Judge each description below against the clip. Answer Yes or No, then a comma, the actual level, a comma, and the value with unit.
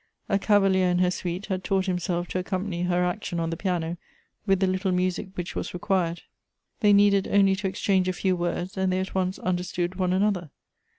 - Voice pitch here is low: No, medium, 185 Hz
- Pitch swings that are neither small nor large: No, narrow, 1.4 semitones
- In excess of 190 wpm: Yes, average, 200 wpm